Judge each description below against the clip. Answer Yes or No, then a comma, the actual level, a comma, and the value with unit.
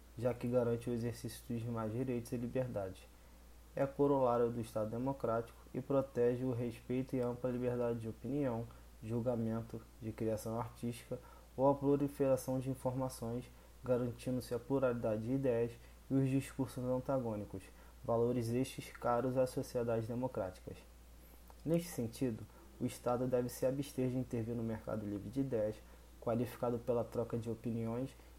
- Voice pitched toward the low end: Yes, low, 120 Hz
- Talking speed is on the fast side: No, average, 140 wpm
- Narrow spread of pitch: Yes, narrow, 2.1 semitones